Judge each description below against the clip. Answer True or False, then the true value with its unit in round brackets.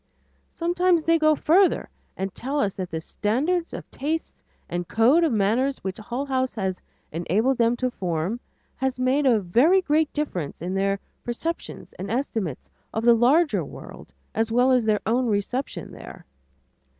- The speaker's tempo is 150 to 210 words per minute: True (165 wpm)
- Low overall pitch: False (245 Hz)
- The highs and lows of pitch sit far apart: True (6.4 semitones)